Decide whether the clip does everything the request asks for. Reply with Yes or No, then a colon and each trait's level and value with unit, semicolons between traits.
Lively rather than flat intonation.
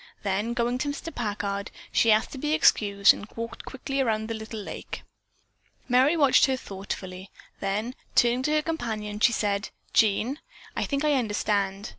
No: average, 4.3 semitones